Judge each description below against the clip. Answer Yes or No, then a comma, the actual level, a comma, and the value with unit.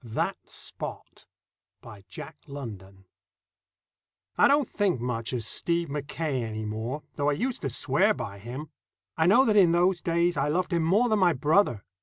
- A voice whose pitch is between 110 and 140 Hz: No, medium, 150 Hz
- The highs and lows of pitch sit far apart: Yes, wide, 7.1 semitones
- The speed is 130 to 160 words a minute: No, average, 170 wpm